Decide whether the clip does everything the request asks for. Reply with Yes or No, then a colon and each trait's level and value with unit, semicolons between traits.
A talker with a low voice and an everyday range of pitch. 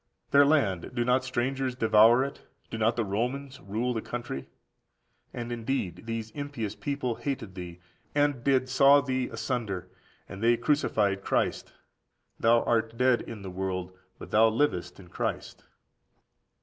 Yes: low, 120 Hz; average, 4.1 semitones